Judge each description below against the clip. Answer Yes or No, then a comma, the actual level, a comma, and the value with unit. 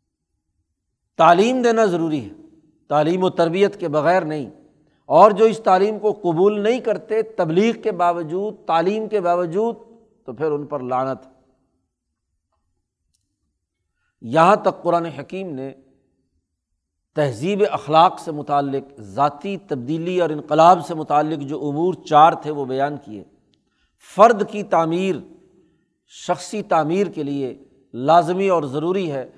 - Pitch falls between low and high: Yes, medium, 165 Hz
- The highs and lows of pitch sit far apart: Yes, wide, 6.0 semitones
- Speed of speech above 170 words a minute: No, average, 125 wpm